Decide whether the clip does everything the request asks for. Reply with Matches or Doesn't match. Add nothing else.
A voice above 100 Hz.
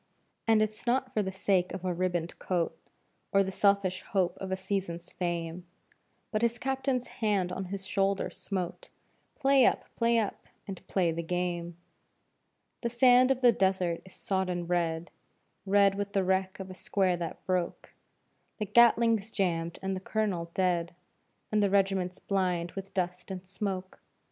Matches